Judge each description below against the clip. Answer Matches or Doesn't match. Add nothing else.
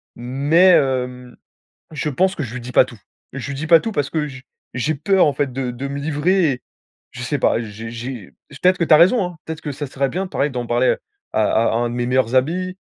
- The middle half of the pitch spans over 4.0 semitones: Matches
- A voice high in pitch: Doesn't match